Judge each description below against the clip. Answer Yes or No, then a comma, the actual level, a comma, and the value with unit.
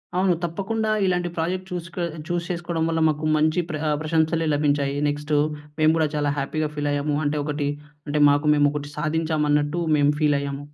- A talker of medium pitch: Yes, medium, 155 Hz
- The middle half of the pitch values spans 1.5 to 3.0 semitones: Yes, narrow, 2.5 semitones